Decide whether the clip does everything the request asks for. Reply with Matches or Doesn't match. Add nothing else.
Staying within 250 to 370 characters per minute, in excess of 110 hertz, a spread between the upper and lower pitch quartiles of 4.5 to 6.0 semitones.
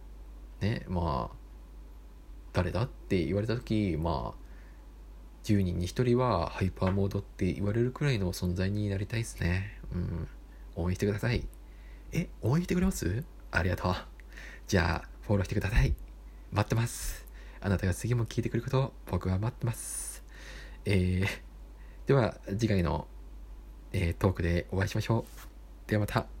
Doesn't match